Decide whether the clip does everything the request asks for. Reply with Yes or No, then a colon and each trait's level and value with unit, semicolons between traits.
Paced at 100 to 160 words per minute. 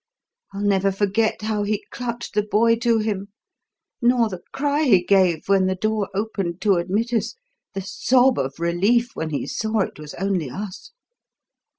No: average, 170 wpm